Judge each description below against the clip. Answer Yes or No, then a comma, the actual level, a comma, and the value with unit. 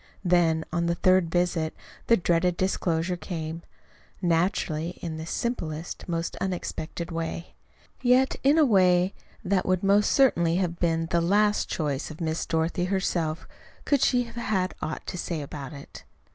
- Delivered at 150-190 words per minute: Yes, average, 160 wpm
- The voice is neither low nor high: Yes, medium, 175 Hz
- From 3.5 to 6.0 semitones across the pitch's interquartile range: No, narrow, 2.5 semitones